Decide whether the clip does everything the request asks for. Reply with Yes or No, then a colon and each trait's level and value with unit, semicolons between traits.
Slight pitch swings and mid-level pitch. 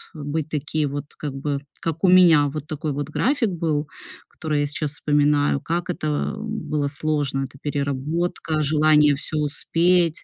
Yes: narrow, 2.1 semitones; medium, 150 Hz